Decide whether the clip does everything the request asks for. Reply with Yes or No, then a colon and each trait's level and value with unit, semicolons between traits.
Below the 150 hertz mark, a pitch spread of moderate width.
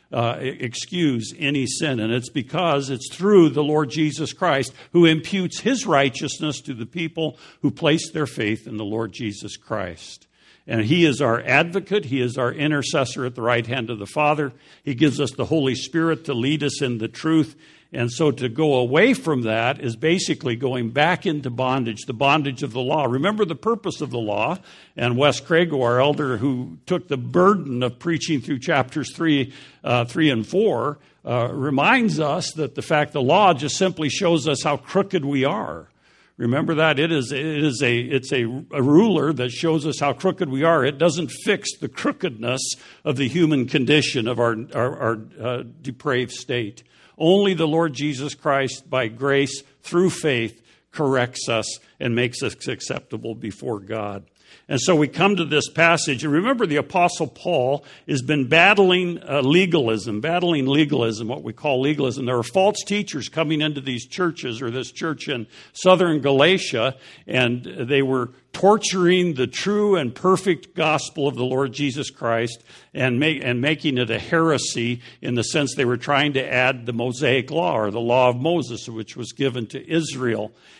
Yes: medium, 140 Hz; average, 4.5 semitones